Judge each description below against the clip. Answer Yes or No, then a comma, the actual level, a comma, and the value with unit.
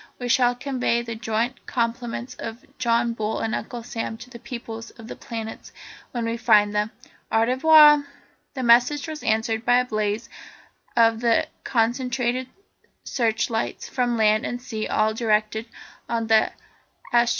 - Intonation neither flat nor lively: No, narrow, 1.8 semitones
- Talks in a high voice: Yes, high, 235 Hz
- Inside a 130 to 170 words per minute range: Yes, average, 150 wpm